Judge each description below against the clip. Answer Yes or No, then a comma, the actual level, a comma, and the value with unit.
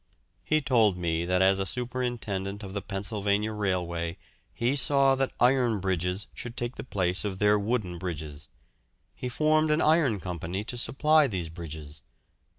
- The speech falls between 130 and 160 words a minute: Yes, average, 155 wpm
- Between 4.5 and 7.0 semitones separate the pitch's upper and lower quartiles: Yes, wide, 5.5 semitones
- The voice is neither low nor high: No, low, 100 Hz